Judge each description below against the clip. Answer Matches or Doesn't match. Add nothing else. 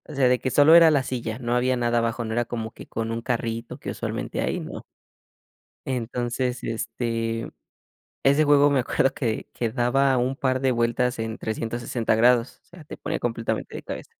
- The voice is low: Matches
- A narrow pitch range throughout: Matches